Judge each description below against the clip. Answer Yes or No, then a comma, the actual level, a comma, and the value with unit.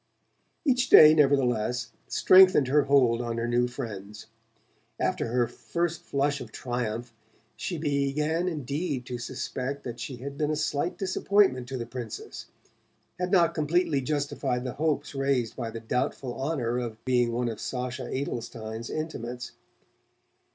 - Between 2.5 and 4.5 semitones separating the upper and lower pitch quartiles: Yes, average, 3.8 semitones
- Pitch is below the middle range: Yes, low, 130 Hz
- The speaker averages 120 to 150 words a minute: Yes, average, 145 wpm